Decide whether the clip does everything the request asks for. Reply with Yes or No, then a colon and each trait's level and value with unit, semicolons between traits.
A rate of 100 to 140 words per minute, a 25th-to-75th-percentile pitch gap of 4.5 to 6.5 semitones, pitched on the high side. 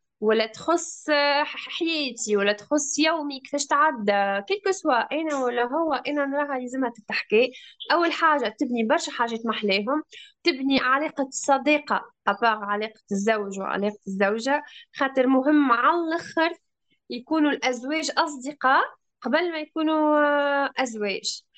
Yes: average, 110 wpm; average, 4.8 semitones; very high, 280 Hz